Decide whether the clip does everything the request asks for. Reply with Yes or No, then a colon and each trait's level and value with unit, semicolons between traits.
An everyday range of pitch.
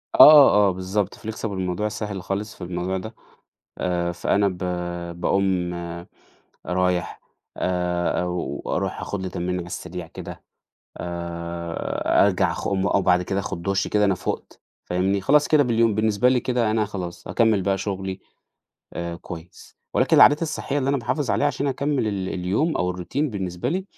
Yes: average, 3.8 semitones